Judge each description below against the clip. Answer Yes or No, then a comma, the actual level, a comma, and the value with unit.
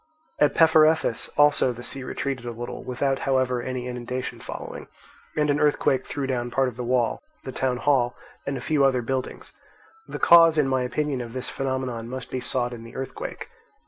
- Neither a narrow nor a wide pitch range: No, narrow, 2.1 semitones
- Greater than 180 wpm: Yes, average, 190 wpm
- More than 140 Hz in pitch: No, low, 130 Hz